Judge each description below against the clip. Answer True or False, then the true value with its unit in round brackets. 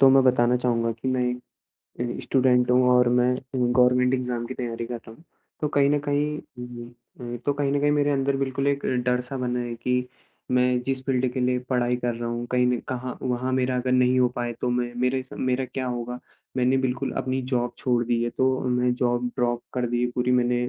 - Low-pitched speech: True (125 Hz)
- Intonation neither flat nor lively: False (1.1 semitones)